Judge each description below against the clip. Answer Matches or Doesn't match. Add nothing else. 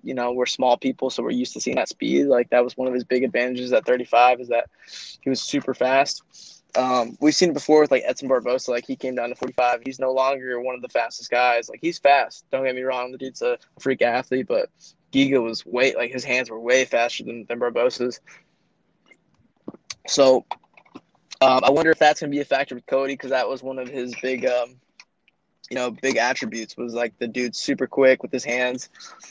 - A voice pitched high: Doesn't match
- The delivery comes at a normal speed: Doesn't match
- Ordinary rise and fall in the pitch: Doesn't match